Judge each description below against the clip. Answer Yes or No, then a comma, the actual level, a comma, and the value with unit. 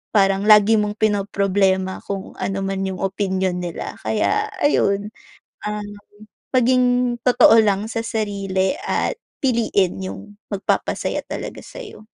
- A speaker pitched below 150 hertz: No, high, 200 Hz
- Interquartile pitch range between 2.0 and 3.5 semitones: Yes, narrow, 2.5 semitones